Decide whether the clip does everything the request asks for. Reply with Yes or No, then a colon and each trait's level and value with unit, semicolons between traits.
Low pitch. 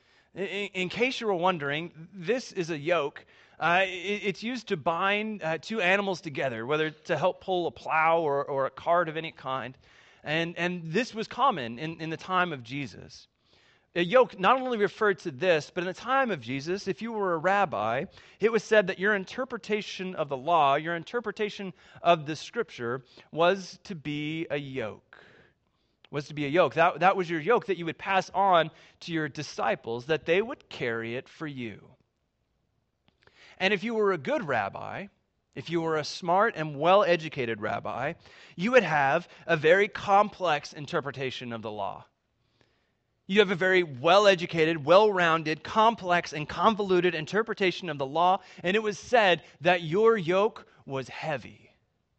No: medium, 175 Hz